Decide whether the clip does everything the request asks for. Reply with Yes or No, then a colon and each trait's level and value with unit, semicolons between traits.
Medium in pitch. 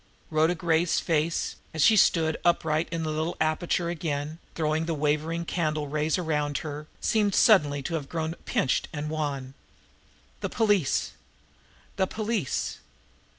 Yes: medium, 160 Hz